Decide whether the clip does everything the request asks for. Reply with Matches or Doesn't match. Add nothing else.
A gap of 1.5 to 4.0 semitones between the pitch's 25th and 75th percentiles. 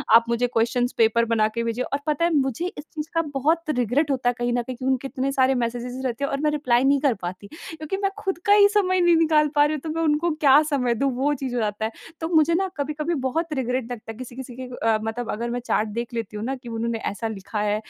Doesn't match